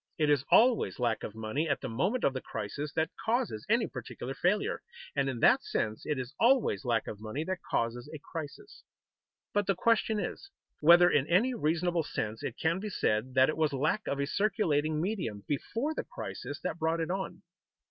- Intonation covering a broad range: Yes, wide, 6.7 semitones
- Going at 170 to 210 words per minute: Yes, average, 200 wpm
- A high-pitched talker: No, medium, 155 Hz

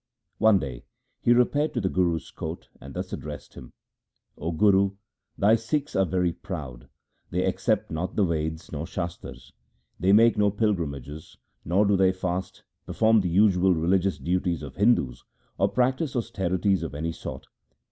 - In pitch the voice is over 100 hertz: No, very low, 95 Hz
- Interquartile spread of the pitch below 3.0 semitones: No, average, 4.3 semitones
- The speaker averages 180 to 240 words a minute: No, average, 160 wpm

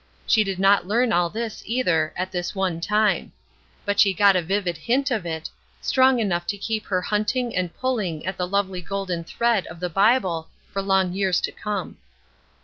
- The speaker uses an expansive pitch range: No, average, 3.2 semitones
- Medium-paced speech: Yes, average, 190 wpm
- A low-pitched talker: No, high, 195 Hz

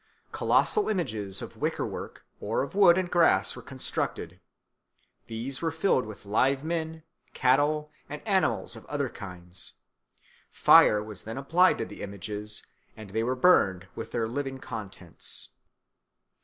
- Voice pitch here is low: Yes, low, 130 Hz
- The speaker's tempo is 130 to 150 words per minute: Yes, average, 140 wpm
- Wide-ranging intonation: Yes, wide, 7.2 semitones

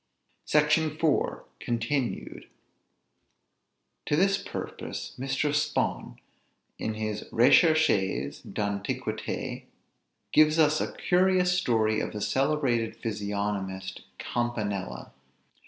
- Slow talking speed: Yes, slow, 85 wpm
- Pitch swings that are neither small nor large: No, wide, 6.8 semitones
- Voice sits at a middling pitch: No, low, 120 Hz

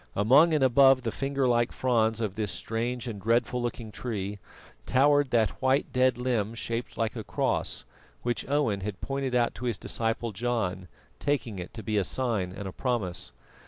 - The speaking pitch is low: Yes, low, 120 Hz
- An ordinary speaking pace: Yes, average, 180 wpm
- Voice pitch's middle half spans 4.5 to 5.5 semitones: No, average, 3.4 semitones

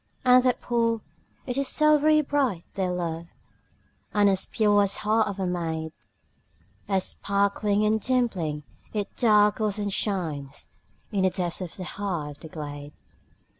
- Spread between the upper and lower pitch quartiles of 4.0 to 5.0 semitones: Yes, average, 4.3 semitones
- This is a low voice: No, high, 200 Hz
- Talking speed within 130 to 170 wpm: Yes, average, 155 wpm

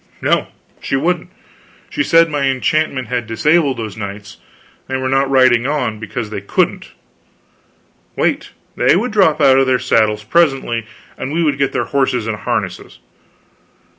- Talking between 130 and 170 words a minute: Yes, average, 160 wpm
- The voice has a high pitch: No, low, 130 Hz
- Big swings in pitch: No, average, 4.8 semitones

